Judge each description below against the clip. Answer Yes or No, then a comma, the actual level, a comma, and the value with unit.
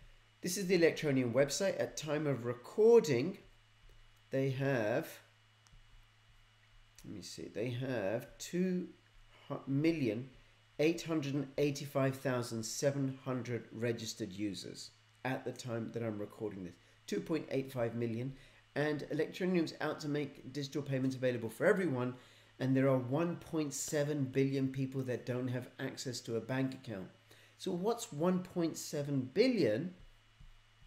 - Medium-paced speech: No, slow, 110 wpm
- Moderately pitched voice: No, low, 130 Hz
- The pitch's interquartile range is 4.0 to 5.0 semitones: Yes, average, 4.4 semitones